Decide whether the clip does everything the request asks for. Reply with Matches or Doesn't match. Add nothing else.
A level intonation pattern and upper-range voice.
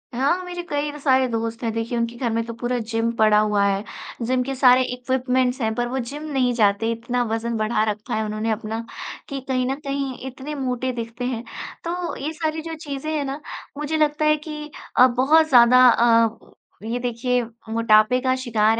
Doesn't match